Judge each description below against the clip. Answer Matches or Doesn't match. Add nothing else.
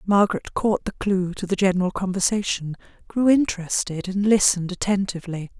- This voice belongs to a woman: Matches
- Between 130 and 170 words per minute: Matches